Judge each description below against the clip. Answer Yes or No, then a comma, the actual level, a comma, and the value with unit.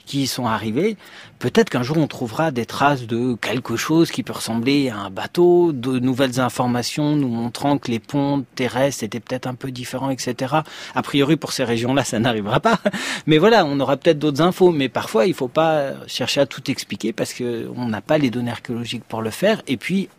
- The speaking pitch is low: Yes, low, 130 Hz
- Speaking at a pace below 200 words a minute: No, average, 210 wpm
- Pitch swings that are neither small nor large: Yes, average, 4.3 semitones